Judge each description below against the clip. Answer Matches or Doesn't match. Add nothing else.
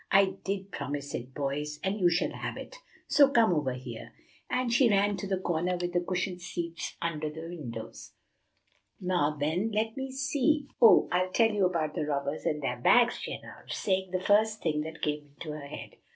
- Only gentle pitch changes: Doesn't match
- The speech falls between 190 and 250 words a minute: Matches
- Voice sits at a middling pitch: Matches